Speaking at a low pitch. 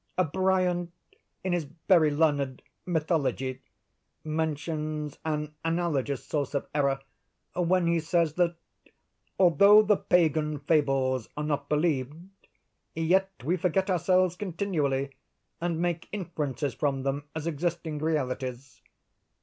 No: medium, 160 Hz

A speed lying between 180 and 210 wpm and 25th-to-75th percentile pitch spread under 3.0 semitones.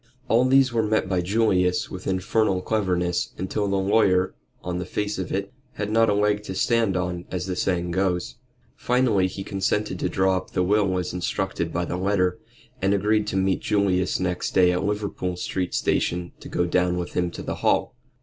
Yes: average, 195 wpm; narrow, 2.5 semitones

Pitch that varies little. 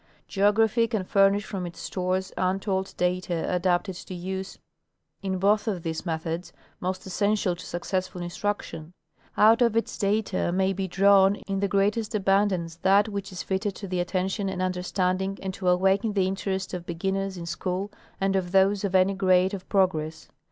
Yes: narrow, 1.7 semitones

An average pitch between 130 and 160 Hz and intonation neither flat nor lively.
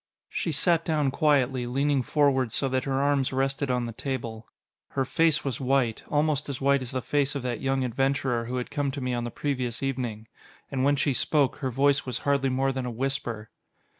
No: low, 135 Hz; narrow, 2.1 semitones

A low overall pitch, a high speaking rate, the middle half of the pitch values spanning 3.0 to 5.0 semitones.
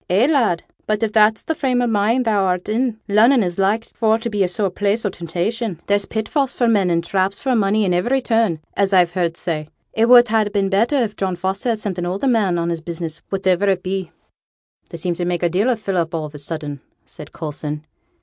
No: high, 195 Hz; fast, 230 wpm; average, 4.2 semitones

